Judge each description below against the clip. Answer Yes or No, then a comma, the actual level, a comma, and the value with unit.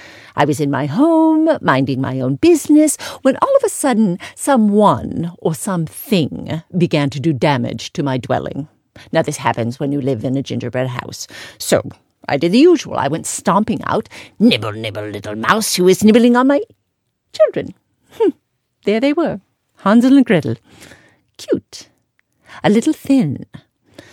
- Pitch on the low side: No, medium, 180 Hz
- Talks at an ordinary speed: Yes, average, 160 wpm